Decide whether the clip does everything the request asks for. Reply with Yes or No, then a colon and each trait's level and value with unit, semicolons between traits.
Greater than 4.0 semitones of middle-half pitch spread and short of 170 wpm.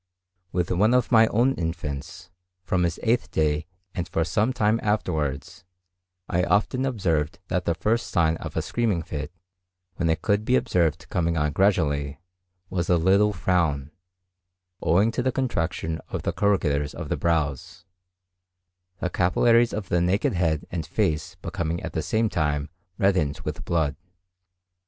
Yes: average, 4.8 semitones; average, 155 wpm